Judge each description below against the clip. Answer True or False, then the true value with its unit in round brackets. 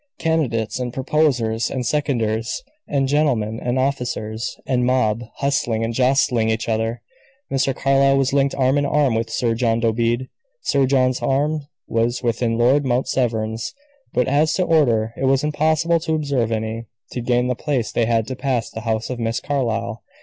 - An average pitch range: True (3.3 semitones)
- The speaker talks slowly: False (170 wpm)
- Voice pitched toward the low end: True (125 Hz)